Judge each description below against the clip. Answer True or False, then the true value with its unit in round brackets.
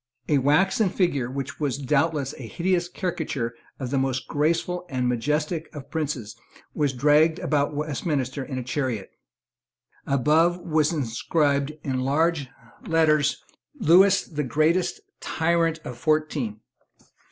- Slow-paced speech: True (125 wpm)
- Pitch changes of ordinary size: True (3.6 semitones)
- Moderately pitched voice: True (150 Hz)